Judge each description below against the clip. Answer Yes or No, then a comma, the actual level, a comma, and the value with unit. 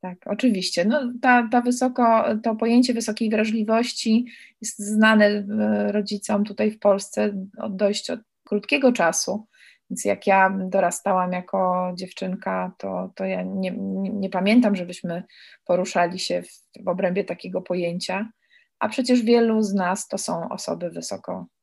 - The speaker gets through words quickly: No, average, 140 wpm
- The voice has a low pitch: No, high, 205 Hz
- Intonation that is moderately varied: Yes, average, 3.6 semitones